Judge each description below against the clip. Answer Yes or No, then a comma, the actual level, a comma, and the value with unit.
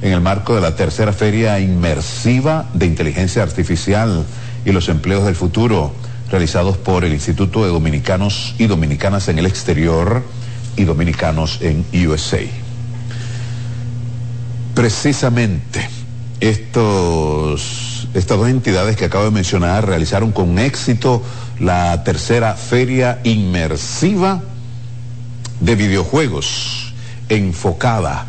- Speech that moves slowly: Yes, slow, 105 wpm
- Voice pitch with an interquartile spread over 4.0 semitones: Yes, average, 4.8 semitones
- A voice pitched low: Yes, low, 110 Hz